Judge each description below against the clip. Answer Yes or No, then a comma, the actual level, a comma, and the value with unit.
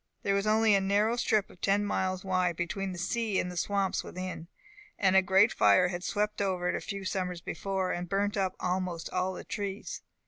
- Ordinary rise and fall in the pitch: No, narrow, 1.8 semitones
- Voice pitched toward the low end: No, high, 190 Hz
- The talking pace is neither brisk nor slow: No, fast, 210 wpm